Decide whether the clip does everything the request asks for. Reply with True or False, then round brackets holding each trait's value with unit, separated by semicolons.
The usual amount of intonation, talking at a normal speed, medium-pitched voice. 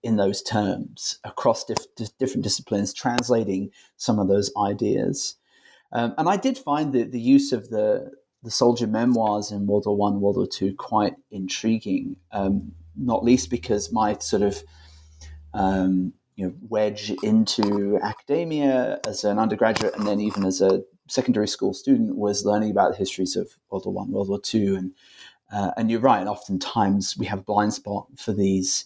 False (3.5 semitones; 175 wpm; 105 Hz)